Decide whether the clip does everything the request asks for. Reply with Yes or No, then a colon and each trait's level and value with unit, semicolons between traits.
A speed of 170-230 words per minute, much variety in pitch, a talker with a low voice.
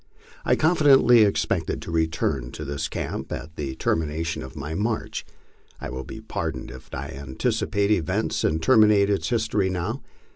No: average, 155 wpm; wide, 6.5 semitones; very low, 85 Hz